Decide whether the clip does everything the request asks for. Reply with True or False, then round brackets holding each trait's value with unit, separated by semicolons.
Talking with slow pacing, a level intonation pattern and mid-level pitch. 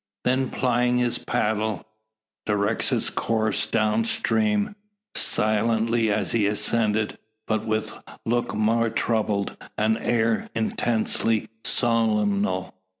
False (100 wpm; 1.5 semitones; 110 Hz)